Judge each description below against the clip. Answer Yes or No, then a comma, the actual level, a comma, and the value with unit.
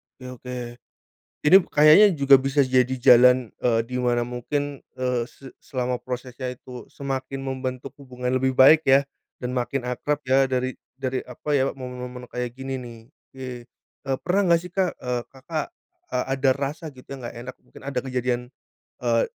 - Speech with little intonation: Yes, narrow, 1.7 semitones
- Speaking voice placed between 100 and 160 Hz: Yes, low, 130 Hz